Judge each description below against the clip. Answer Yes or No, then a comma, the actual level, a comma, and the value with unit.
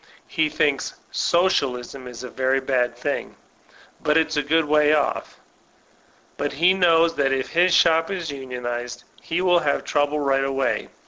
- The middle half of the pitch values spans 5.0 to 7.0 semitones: No, average, 3.6 semitones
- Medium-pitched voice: Yes, medium, 145 Hz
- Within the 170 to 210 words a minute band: No, average, 155 wpm